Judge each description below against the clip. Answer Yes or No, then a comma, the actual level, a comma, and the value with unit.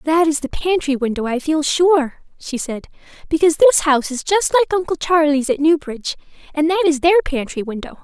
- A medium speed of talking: Yes, average, 195 wpm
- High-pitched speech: Yes, very high, 310 Hz